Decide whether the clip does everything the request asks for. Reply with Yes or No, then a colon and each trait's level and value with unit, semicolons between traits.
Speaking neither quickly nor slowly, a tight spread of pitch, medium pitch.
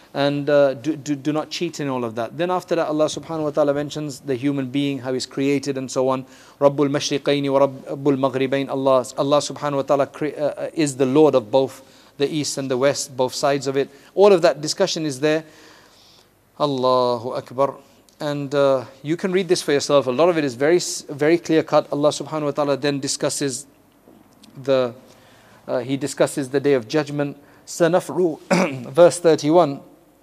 Yes: average, 180 wpm; narrow, 2.2 semitones; medium, 145 Hz